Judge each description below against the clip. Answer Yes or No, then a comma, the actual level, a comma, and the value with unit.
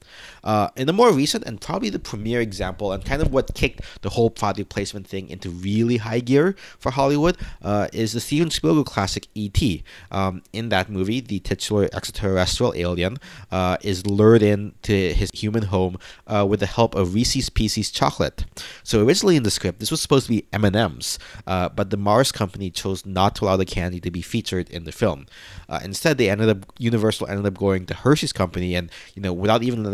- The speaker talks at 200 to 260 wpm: Yes, fast, 205 wpm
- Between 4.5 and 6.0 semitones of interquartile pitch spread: No, average, 3.2 semitones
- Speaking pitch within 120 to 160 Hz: No, low, 100 Hz